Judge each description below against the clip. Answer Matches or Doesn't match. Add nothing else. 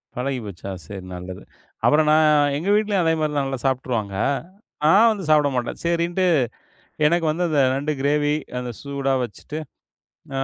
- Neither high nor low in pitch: Matches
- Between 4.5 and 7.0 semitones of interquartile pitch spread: Matches